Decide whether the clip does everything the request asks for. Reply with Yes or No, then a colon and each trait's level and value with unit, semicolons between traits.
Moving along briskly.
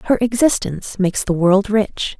No: average, 165 wpm